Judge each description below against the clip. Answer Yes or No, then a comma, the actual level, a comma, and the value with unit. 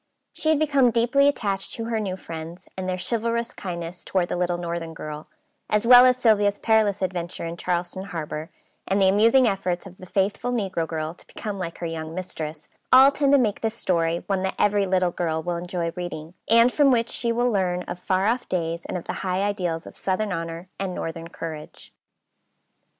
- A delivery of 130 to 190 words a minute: No, average, 200 wpm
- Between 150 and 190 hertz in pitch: Yes, medium, 185 Hz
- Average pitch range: Yes, average, 4.6 semitones